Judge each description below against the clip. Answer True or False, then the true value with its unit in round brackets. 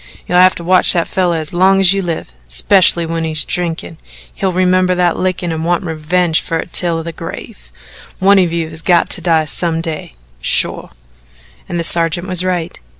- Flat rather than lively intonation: True (2.0 semitones)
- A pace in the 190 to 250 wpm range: True (195 wpm)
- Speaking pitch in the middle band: True (170 Hz)